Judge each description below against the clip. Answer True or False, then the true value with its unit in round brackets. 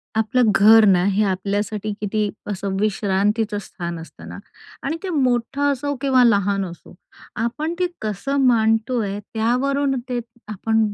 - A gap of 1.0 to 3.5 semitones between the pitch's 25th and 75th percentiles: False (3.9 semitones)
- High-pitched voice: True (220 Hz)